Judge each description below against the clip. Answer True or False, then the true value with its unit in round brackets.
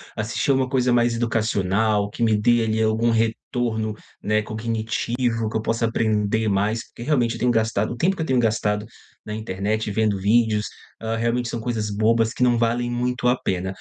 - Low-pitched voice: True (115 Hz)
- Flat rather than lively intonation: True (1.8 semitones)